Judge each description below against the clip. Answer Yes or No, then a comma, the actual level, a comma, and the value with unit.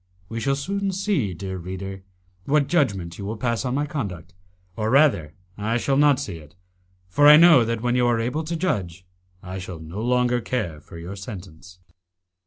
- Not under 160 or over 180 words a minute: No, average, 190 wpm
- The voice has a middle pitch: No, low, 115 Hz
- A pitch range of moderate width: No, wide, 7.0 semitones